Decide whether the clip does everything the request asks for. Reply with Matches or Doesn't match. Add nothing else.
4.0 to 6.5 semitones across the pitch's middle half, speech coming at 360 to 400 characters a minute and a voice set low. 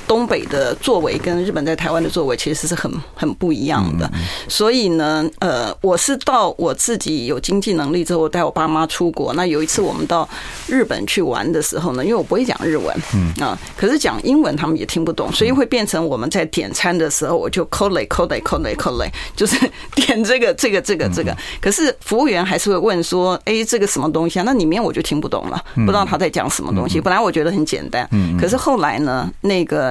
Doesn't match